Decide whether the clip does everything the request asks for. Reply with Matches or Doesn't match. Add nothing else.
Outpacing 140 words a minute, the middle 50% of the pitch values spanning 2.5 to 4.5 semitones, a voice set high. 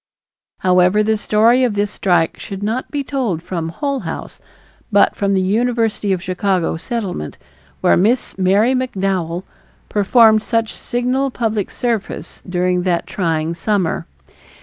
Doesn't match